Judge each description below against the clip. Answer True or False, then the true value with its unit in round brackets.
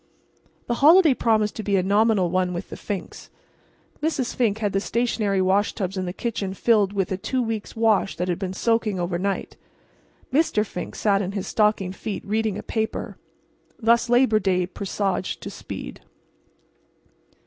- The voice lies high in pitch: True (205 Hz)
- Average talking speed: True (160 wpm)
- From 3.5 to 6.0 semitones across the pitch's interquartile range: False (3.1 semitones)